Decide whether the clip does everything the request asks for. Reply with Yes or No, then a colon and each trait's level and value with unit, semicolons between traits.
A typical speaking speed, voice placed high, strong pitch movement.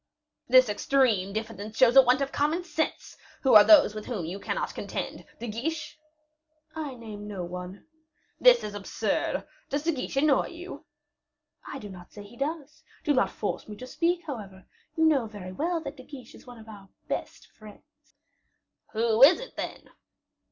Yes: average, 180 wpm; very high, 250 Hz; wide, 6.4 semitones